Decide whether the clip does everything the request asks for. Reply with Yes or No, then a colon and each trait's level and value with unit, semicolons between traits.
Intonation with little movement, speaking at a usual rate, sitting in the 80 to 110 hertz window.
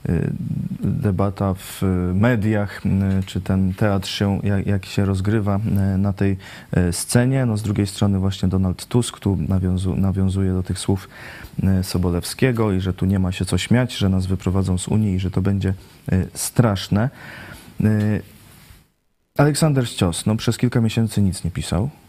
Yes: narrow, 2.1 semitones; average, 150 wpm; low, 100 Hz